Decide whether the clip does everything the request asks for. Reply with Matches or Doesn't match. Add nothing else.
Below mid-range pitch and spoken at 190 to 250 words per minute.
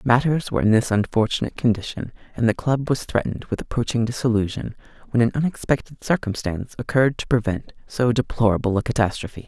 Doesn't match